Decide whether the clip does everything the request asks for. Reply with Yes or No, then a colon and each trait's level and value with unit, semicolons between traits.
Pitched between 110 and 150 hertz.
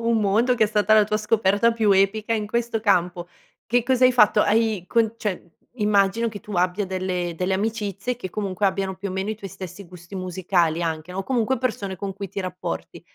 No: high, 200 Hz